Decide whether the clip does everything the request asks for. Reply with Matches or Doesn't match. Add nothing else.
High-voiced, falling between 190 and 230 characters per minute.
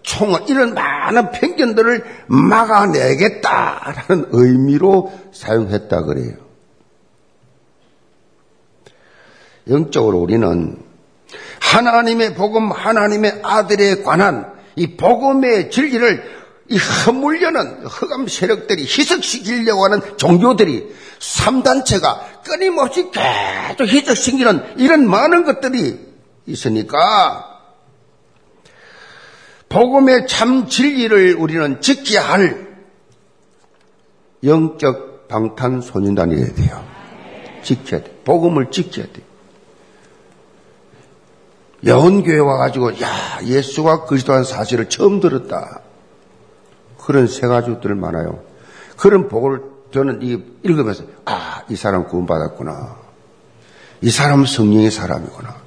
Matches